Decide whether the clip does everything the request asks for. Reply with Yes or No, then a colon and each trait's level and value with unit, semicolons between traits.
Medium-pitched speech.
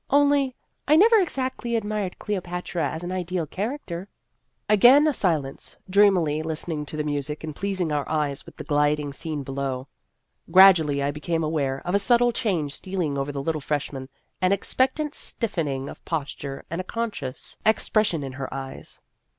Yes: medium, 165 Hz